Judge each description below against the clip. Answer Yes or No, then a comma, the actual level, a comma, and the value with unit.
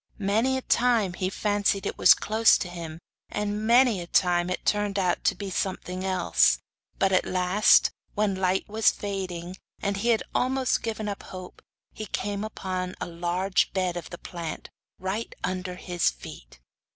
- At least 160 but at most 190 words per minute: Yes, average, 165 wpm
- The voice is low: No, high, 190 Hz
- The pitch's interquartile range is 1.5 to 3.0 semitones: Yes, narrow, 2.5 semitones